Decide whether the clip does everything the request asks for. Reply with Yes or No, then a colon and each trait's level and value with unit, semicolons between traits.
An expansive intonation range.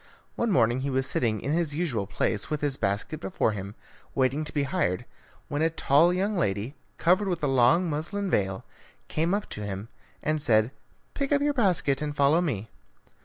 Yes: wide, 7.3 semitones